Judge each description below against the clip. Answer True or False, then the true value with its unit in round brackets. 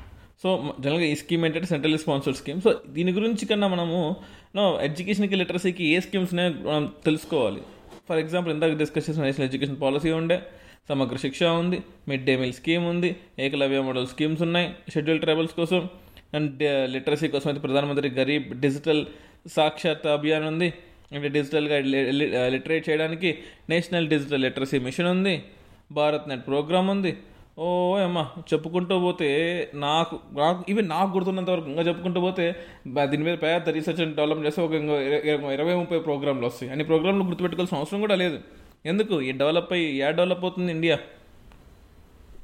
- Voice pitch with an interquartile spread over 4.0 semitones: False (3.6 semitones)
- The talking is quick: True (150 wpm)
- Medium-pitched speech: True (160 Hz)